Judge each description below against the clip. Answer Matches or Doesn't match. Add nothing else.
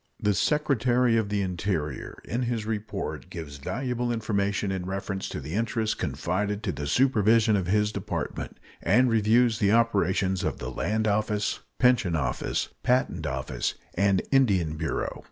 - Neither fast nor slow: Matches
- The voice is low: Matches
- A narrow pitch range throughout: Doesn't match